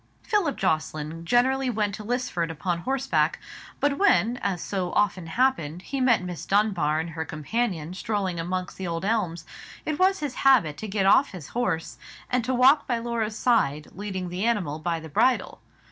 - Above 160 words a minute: Yes, average, 175 wpm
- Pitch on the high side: Yes, high, 200 Hz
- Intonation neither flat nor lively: No, wide, 6.6 semitones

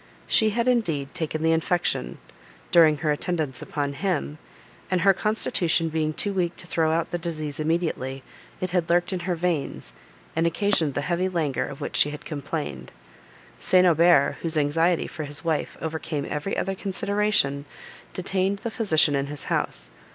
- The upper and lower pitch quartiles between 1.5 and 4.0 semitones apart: Yes, average, 3.6 semitones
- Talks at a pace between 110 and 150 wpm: No, average, 165 wpm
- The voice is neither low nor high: Yes, medium, 165 Hz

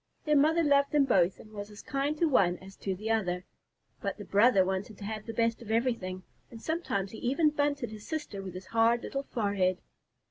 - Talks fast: Yes, fast, 215 wpm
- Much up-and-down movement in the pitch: Yes, wide, 6.1 semitones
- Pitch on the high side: Yes, high, 220 Hz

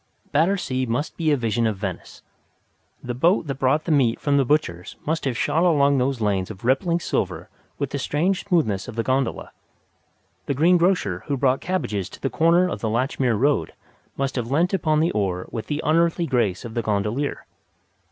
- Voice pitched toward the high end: No, low, 135 Hz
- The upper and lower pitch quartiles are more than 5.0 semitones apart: Yes, wide, 5.6 semitones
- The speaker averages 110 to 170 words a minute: No, average, 190 wpm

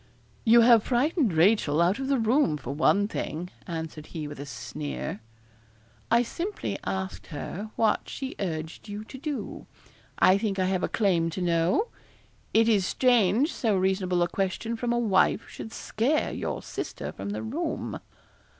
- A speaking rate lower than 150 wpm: No, average, 165 wpm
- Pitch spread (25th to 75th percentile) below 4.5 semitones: No, wide, 5.4 semitones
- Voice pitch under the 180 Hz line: No, high, 205 Hz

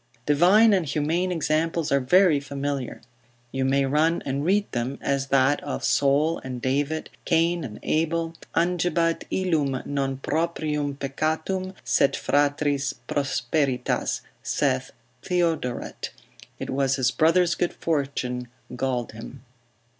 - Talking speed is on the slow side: Yes, slow, 120 wpm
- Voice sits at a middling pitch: Yes, medium, 145 Hz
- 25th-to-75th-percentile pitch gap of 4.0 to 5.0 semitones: No, average, 3.5 semitones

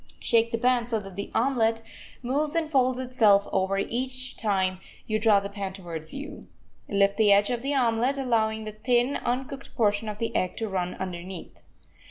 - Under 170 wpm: No, average, 185 wpm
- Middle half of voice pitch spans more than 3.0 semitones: Yes, average, 4.0 semitones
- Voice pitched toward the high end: Yes, high, 225 Hz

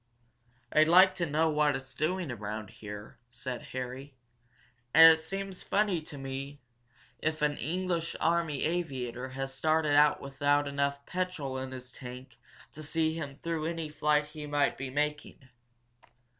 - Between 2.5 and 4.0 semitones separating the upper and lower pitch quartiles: Yes, average, 3.3 semitones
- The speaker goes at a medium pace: Yes, average, 150 wpm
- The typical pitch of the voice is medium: Yes, medium, 145 Hz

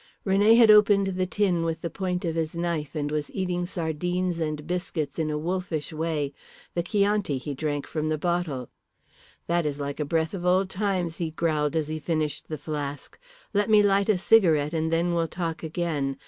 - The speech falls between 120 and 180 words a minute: No, average, 195 wpm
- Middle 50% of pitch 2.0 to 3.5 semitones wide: Yes, average, 3.2 semitones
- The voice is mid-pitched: Yes, medium, 165 Hz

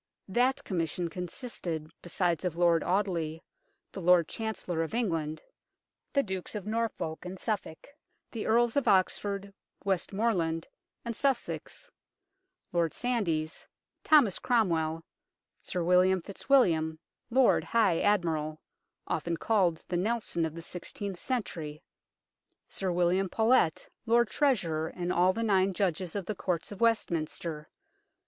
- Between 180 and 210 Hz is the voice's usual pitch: Yes, medium, 185 Hz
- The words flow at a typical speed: No, slow, 125 wpm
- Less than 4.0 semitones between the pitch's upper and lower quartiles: No, average, 4.9 semitones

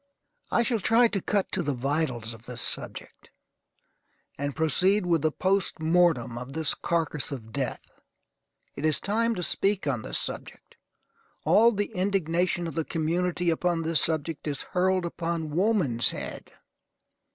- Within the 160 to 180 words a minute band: No, average, 150 wpm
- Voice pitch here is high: No, medium, 165 Hz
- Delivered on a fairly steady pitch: No, average, 4.4 semitones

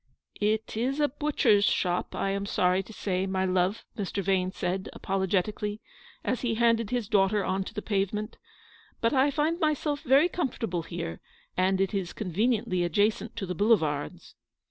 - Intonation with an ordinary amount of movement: Yes, average, 3.6 semitones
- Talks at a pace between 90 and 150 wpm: No, average, 170 wpm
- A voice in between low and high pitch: No, high, 205 Hz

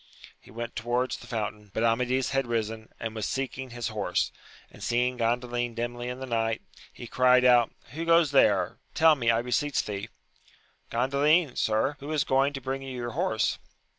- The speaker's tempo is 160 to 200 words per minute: Yes, average, 190 wpm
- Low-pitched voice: Yes, low, 120 Hz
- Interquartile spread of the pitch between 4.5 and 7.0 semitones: No, average, 2.7 semitones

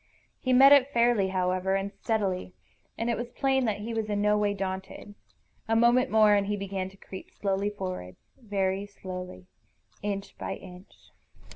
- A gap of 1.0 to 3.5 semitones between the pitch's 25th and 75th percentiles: Yes, average, 2.9 semitones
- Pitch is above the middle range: Yes, high, 205 Hz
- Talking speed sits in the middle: Yes, average, 170 wpm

